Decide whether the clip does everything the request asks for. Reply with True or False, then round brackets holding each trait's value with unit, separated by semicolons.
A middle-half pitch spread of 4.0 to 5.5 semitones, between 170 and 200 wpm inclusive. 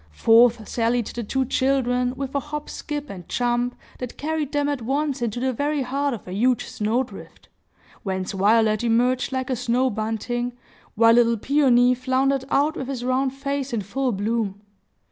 False (2.9 semitones; 175 wpm)